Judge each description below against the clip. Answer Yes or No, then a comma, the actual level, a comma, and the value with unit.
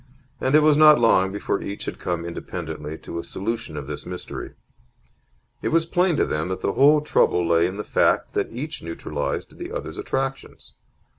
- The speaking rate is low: No, average, 190 wpm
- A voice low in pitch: Yes, low, 100 Hz